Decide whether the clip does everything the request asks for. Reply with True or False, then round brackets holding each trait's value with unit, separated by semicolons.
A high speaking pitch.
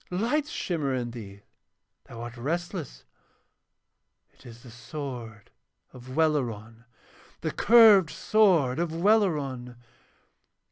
False (135 Hz)